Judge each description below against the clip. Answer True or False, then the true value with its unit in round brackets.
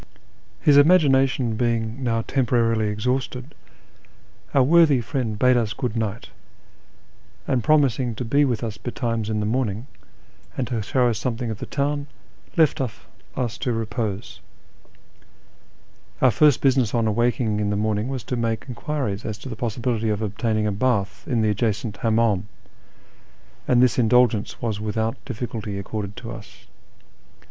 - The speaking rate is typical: True (150 wpm)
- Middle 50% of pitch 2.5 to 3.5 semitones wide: True (3.0 semitones)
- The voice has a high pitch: False (115 Hz)